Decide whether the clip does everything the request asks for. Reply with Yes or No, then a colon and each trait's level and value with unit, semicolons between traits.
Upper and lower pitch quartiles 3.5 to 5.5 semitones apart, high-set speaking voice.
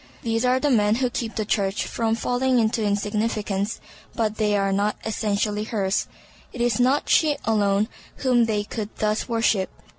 No: narrow, 2.4 semitones; high, 220 Hz